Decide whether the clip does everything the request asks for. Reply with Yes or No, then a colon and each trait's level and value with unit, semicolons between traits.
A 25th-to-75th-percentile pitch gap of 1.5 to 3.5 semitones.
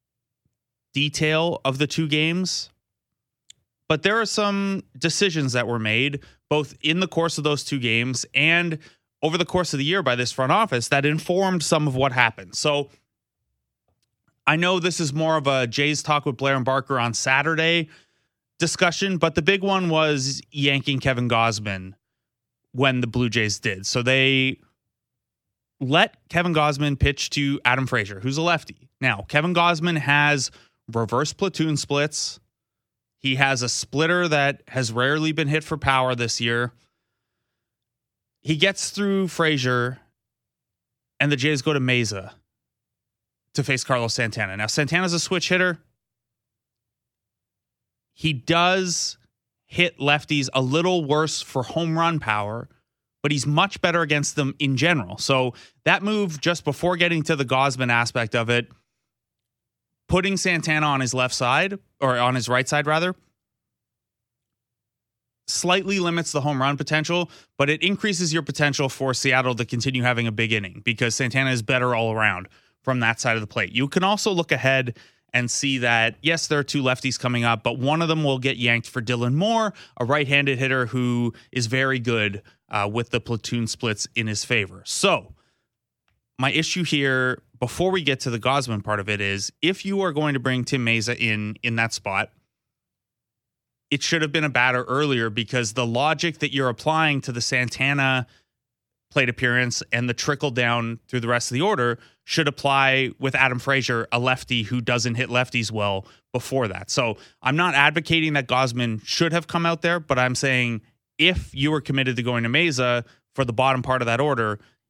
No: average, 4.3 semitones